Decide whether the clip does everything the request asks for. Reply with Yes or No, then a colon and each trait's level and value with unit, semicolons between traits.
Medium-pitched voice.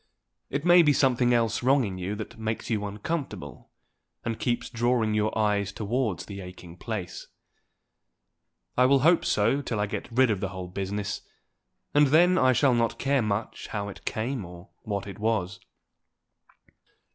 No: low, 110 Hz